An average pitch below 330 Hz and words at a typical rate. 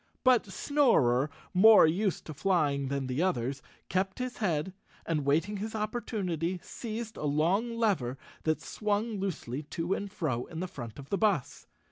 Yes: medium, 185 Hz; average, 160 wpm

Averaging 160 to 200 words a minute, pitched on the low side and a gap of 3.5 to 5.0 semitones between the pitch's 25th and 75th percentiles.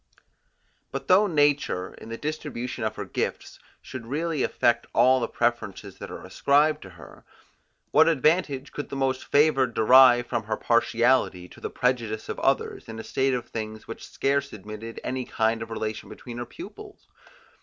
Yes: average, 170 wpm; low, 125 Hz; average, 3.8 semitones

